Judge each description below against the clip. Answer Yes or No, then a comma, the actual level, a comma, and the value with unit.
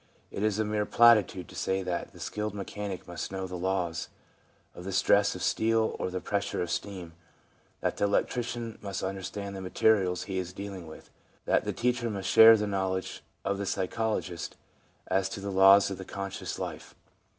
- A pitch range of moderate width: No, narrow, 2.0 semitones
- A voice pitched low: Yes, low, 100 Hz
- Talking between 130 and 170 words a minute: No, average, 190 wpm